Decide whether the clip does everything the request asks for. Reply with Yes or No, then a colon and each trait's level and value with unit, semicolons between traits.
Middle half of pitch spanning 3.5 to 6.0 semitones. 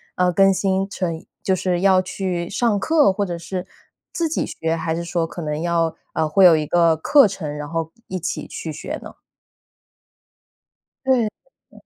No: average, 2.9 semitones